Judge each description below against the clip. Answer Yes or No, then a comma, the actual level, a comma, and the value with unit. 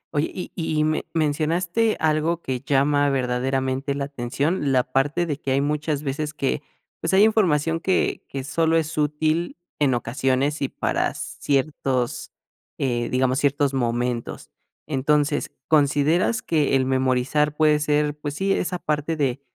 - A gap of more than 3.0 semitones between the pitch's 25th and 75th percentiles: No, average, 2.7 semitones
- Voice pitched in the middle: Yes, medium, 145 Hz